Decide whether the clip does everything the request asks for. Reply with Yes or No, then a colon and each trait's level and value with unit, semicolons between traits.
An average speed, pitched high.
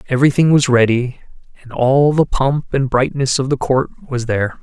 No: average, 180 wpm; low, 130 Hz